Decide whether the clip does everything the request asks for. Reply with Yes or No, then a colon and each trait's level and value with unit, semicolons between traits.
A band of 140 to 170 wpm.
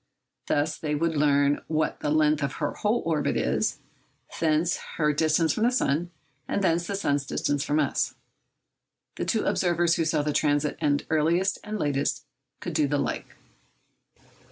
Yes: average, 165 wpm